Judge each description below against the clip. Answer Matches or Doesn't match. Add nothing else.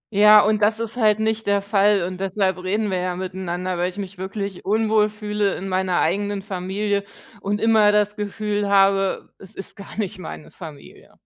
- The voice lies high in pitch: Matches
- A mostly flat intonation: Matches